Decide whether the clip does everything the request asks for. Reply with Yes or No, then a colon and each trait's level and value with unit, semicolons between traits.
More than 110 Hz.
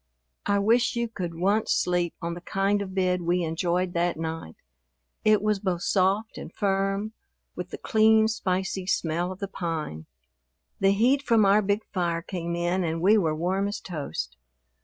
Yes: medium, 185 Hz